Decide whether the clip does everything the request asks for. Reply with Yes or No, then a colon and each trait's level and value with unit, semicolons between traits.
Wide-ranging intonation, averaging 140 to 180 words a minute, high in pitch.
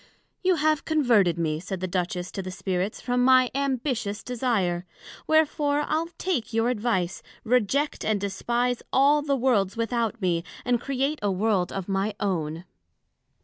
Yes: wide, 5.8 semitones; average, 150 wpm; high, 230 Hz